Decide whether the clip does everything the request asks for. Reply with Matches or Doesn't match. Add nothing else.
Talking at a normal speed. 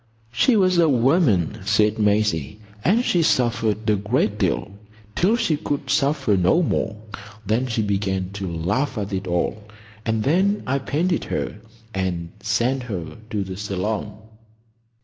Matches